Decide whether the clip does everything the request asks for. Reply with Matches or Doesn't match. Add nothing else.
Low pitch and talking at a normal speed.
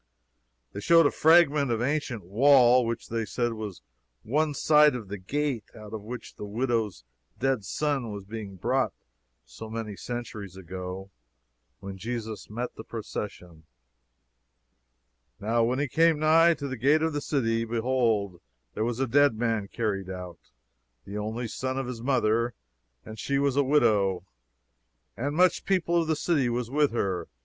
Matches